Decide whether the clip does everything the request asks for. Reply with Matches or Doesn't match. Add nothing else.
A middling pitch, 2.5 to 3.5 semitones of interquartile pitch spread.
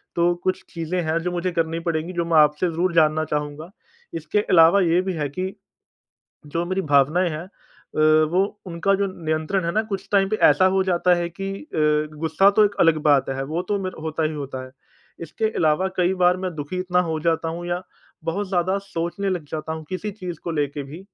Matches